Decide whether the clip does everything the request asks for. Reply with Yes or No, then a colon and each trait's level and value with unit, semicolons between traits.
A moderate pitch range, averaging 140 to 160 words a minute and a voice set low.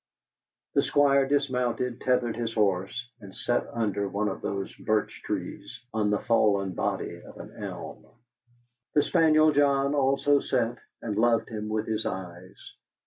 Yes: average, 4.8 semitones; average, 145 wpm; low, 115 Hz